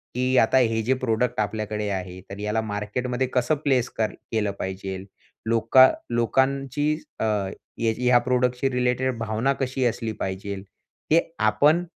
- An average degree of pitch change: Yes, average, 3.4 semitones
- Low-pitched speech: Yes, low, 115 Hz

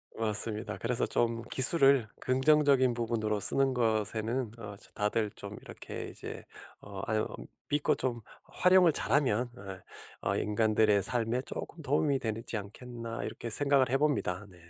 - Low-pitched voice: Yes, low, 115 Hz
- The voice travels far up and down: No, average, 3.6 semitones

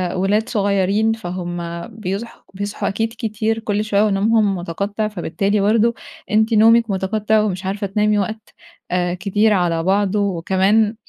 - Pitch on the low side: No, high, 205 Hz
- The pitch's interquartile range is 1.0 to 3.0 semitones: Yes, narrow, 2.4 semitones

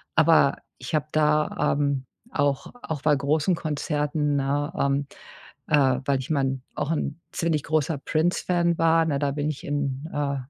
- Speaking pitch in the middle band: Yes, medium, 145 Hz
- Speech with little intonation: Yes, narrow, 2.0 semitones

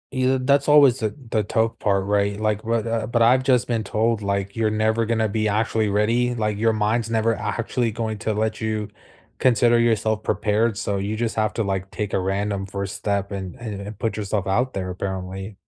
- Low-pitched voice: Yes, low, 110 Hz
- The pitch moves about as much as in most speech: No, narrow, 2.3 semitones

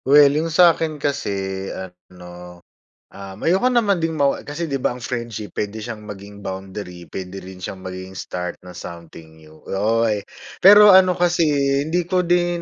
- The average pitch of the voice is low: Yes, low, 110 Hz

